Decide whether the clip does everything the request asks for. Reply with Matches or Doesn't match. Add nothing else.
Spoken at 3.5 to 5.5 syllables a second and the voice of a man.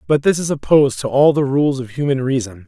Doesn't match